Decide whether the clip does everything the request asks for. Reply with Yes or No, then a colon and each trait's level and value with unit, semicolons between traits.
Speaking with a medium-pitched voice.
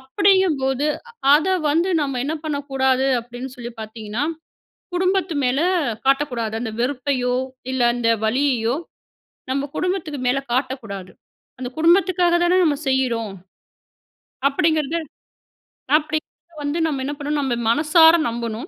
No: very high, 275 Hz